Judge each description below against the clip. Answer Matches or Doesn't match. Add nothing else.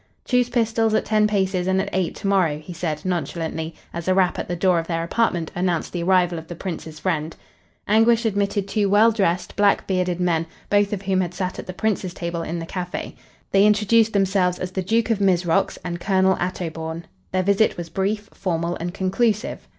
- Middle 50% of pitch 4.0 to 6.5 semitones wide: Doesn't match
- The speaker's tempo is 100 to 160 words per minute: Doesn't match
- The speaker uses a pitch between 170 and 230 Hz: Matches